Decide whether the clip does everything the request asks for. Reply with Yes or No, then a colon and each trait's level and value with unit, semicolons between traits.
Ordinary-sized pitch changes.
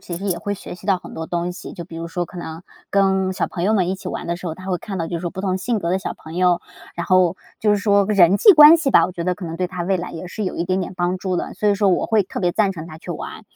No: narrow, 2.2 semitones